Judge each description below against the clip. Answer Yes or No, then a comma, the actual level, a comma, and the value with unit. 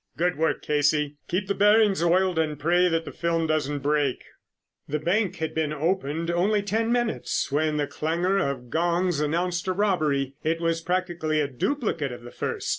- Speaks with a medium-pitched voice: Yes, medium, 165 Hz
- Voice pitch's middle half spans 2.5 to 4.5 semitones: Yes, average, 3.6 semitones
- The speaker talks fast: No, average, 180 wpm